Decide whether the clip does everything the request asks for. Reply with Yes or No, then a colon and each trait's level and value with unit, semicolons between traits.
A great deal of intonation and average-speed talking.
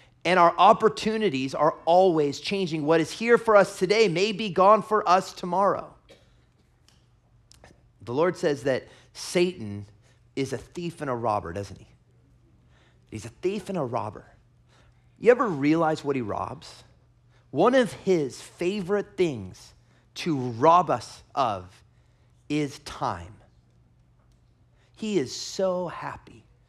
No: wide, 7.7 semitones; slow, 130 wpm